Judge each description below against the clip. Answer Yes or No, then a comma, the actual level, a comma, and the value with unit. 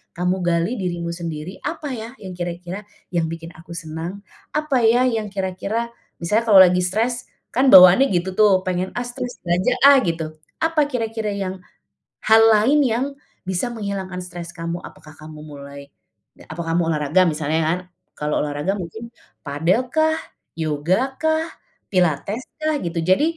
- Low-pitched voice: No, medium, 185 Hz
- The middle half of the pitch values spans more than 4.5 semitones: Yes, average, 5.3 semitones